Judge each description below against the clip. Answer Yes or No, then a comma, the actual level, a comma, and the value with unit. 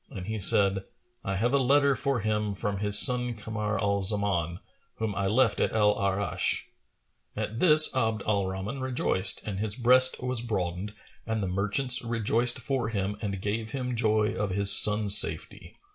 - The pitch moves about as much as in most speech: Yes, average, 3.3 semitones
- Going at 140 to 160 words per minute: No, average, 175 wpm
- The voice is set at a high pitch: No, low, 105 Hz